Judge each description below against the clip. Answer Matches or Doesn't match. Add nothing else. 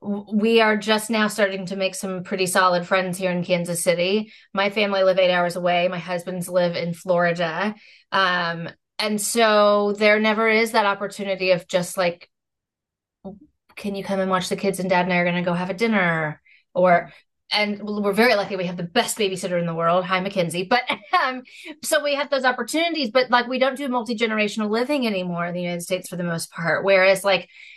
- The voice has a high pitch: Matches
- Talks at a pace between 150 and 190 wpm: Doesn't match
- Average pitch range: Matches